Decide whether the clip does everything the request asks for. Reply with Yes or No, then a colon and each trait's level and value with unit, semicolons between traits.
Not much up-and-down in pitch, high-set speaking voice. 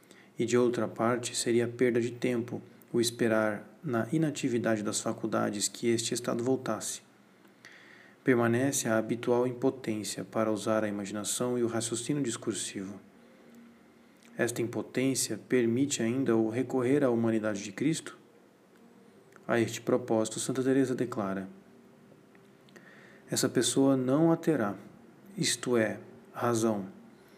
No: narrow, 2.3 semitones; low, 115 Hz